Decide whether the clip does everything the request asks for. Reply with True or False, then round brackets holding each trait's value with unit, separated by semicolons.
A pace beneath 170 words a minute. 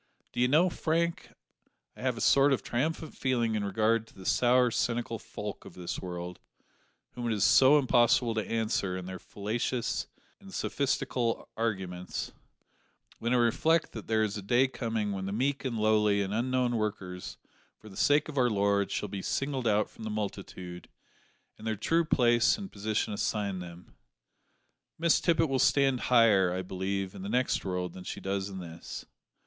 False (175 wpm)